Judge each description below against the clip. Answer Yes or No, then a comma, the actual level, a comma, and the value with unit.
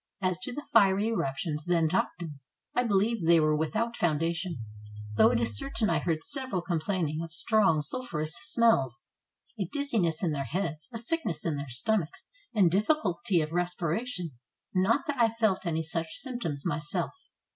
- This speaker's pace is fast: No, average, 165 wpm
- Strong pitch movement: Yes, wide, 6.0 semitones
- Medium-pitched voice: Yes, medium, 175 Hz